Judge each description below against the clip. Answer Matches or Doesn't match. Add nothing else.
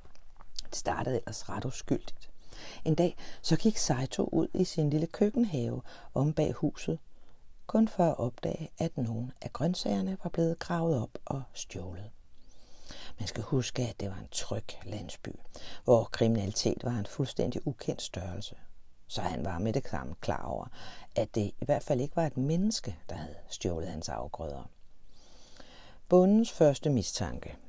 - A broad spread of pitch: Matches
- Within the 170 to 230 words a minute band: Doesn't match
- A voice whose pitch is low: Matches